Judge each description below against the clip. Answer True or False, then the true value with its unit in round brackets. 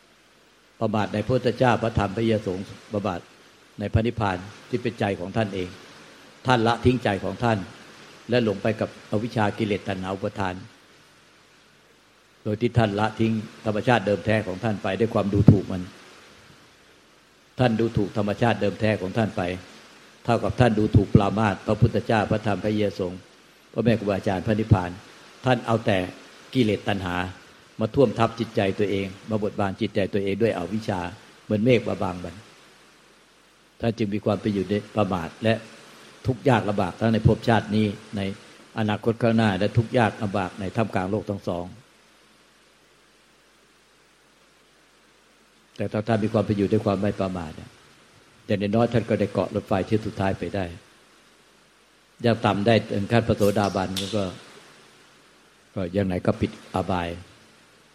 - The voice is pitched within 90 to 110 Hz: True (105 Hz)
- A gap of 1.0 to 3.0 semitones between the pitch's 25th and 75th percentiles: True (2.5 semitones)